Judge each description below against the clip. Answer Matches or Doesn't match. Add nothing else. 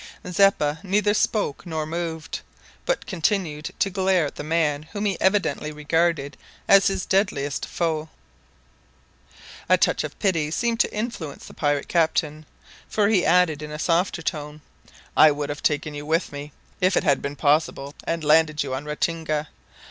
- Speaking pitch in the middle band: Matches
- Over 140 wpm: Matches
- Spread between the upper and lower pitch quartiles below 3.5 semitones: Doesn't match